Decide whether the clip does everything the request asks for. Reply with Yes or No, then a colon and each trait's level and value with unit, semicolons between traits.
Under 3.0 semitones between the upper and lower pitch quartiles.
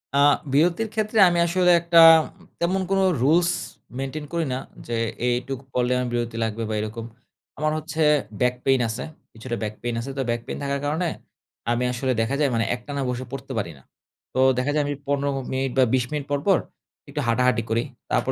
No: average, 4.4 semitones